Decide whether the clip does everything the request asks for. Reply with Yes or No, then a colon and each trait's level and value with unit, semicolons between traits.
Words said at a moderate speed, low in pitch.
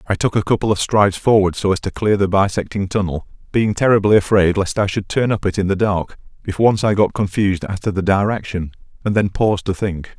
No: fast, 235 wpm; low, 100 Hz